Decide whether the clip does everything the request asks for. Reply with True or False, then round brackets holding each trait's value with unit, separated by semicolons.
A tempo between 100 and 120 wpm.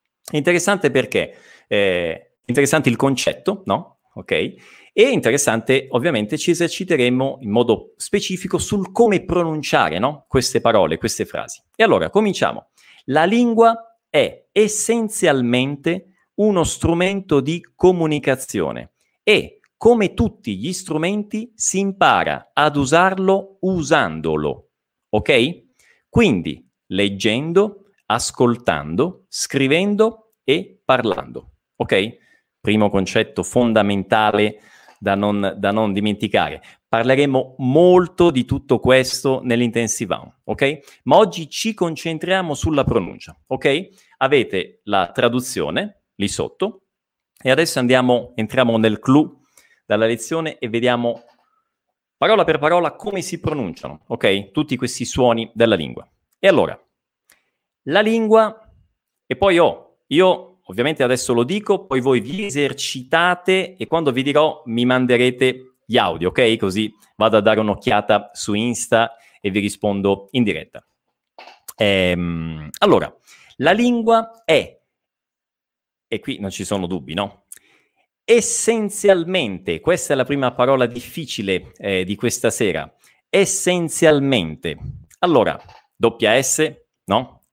True (115 wpm)